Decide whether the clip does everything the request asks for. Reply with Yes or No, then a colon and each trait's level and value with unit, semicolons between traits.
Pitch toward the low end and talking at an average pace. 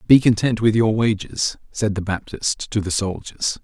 Yes: low, 105 Hz; average, 180 wpm